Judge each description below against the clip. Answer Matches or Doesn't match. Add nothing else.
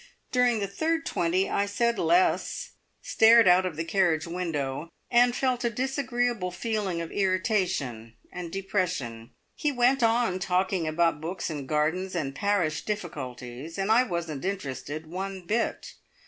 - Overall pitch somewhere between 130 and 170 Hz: Doesn't match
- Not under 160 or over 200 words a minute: Doesn't match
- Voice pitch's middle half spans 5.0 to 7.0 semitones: Matches